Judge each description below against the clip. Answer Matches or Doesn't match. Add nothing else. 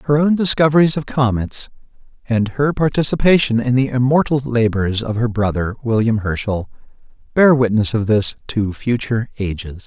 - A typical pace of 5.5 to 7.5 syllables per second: Doesn't match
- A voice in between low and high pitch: Doesn't match